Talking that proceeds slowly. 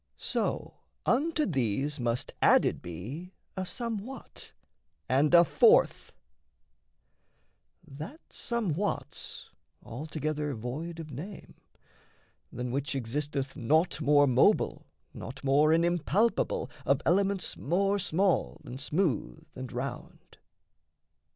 Yes: slow, 100 wpm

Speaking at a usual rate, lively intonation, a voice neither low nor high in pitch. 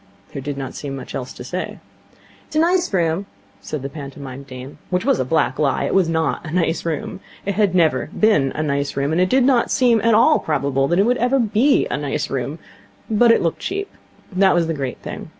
No: fast, 230 wpm; wide, 7.4 semitones; medium, 165 Hz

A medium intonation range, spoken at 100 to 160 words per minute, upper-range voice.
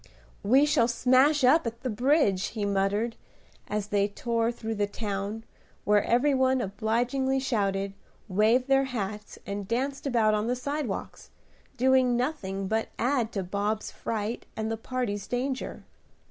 Yes: average, 4.0 semitones; average, 145 wpm; high, 230 Hz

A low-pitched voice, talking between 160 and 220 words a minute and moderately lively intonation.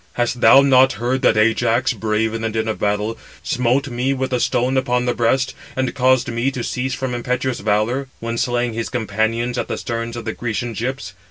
No: low, 120 Hz; fast, 205 wpm; narrow, 2.3 semitones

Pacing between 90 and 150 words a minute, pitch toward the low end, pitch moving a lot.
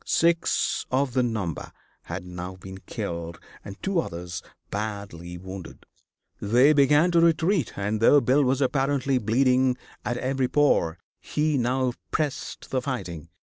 Yes: average, 140 wpm; low, 125 Hz; wide, 6.8 semitones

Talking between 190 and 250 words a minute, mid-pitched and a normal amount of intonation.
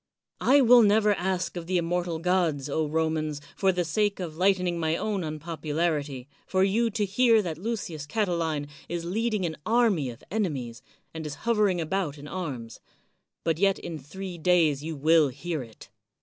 No: average, 175 wpm; medium, 170 Hz; average, 4.1 semitones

